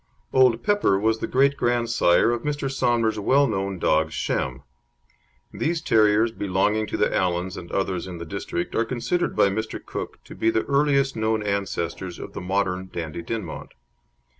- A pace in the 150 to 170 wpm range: Yes, average, 165 wpm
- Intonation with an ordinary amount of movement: Yes, average, 4.5 semitones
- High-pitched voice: No, low, 110 Hz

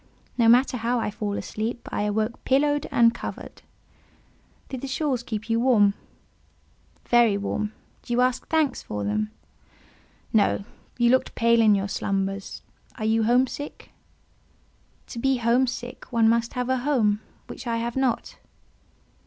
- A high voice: Yes, high, 235 Hz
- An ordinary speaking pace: Yes, average, 155 wpm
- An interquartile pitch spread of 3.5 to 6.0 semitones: No, average, 2.8 semitones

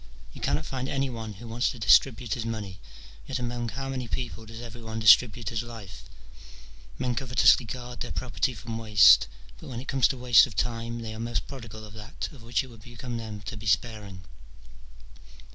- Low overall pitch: Yes, low, 115 Hz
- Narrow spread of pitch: Yes, narrow, 2.1 semitones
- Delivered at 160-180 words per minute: No, average, 200 wpm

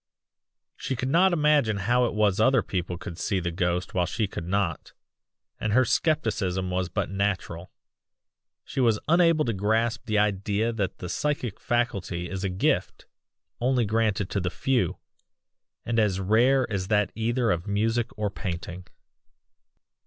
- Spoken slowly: No, average, 155 wpm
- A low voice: Yes, low, 105 Hz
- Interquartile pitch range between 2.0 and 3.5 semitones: No, average, 4.3 semitones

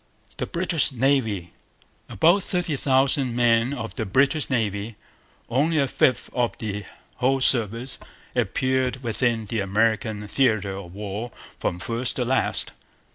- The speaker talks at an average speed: No, slow, 130 wpm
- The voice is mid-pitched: No, low, 120 Hz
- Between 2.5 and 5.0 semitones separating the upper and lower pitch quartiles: Yes, average, 3.8 semitones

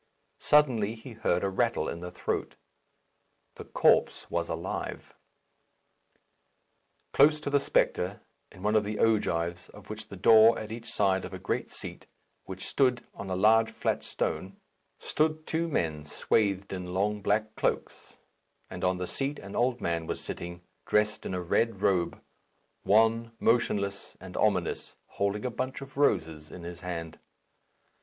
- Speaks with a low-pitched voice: Yes, low, 105 Hz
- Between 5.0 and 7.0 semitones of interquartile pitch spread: No, average, 4.1 semitones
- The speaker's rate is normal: Yes, average, 155 wpm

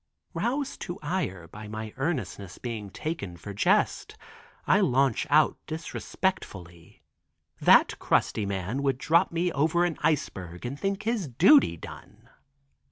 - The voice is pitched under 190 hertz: Yes, low, 135 Hz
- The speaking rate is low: Yes, slow, 130 wpm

